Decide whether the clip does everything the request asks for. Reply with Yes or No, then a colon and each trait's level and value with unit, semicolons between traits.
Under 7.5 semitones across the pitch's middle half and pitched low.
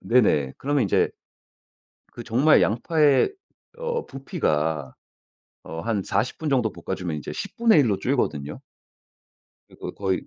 No: wide, 8.8 semitones; low, 115 Hz